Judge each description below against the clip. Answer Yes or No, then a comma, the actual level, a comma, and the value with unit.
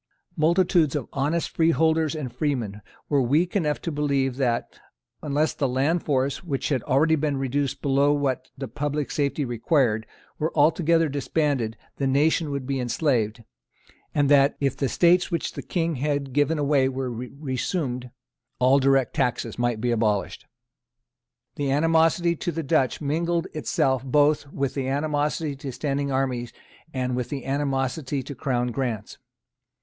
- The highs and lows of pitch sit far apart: No, average, 2.8 semitones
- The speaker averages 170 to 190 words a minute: No, average, 150 wpm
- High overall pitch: No, medium, 140 Hz